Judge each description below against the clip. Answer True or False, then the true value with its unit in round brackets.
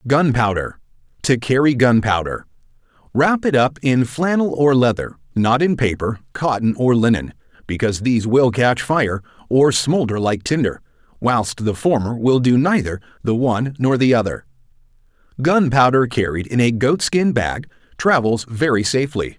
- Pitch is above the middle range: False (125 Hz)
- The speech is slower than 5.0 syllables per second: True (4.8 syllables/s)